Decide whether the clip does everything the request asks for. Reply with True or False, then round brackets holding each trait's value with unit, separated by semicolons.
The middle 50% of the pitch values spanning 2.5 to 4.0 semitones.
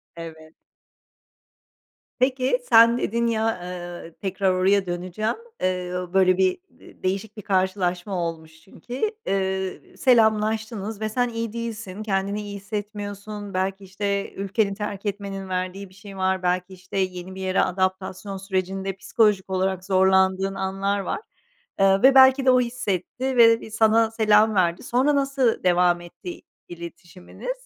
True (2.9 semitones)